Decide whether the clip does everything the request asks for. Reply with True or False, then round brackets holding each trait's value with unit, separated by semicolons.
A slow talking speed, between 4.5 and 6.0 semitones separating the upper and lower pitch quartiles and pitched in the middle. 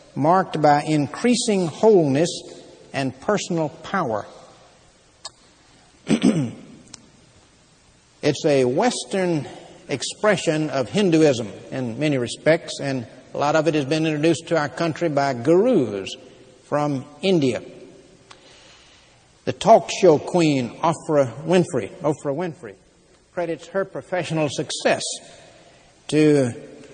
False (100 wpm; 3.8 semitones; 155 Hz)